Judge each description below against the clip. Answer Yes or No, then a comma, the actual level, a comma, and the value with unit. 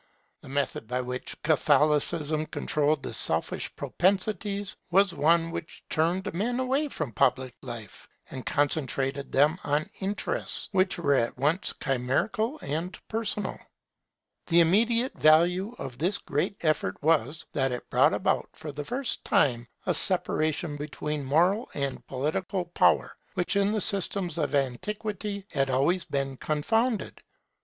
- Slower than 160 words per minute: Yes, slow, 135 wpm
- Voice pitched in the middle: Yes, medium, 160 Hz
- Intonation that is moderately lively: No, wide, 5.8 semitones